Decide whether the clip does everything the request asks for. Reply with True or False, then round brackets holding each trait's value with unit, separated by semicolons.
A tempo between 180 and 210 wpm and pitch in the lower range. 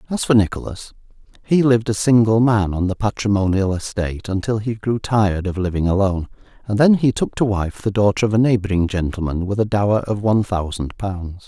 True (200 wpm; 105 Hz)